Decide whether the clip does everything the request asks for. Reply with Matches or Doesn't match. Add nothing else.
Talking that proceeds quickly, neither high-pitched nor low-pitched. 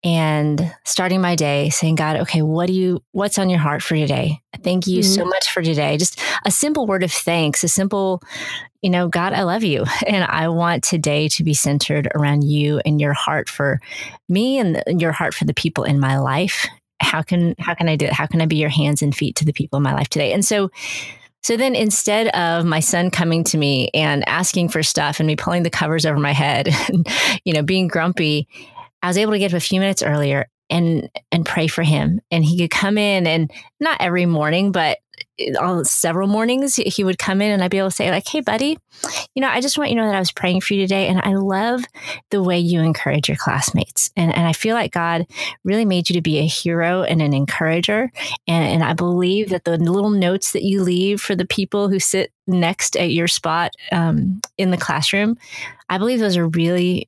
Matches